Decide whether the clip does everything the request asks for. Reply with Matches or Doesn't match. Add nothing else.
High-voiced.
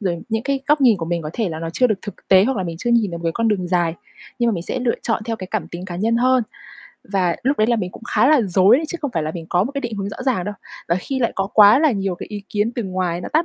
Matches